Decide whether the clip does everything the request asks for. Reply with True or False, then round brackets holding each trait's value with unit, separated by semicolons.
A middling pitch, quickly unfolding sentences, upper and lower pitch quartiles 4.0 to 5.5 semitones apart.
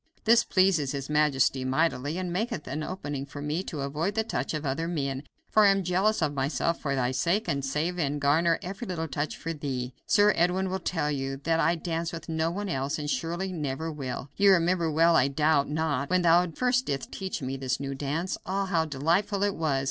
True (160 Hz; 215 wpm; 4.4 semitones)